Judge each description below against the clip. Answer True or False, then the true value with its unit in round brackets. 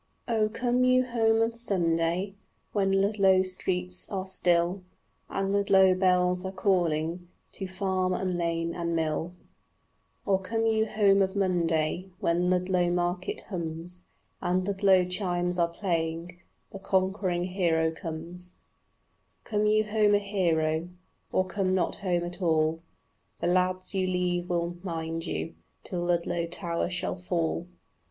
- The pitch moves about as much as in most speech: False (2.1 semitones)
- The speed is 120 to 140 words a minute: True (135 wpm)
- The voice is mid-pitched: True (180 Hz)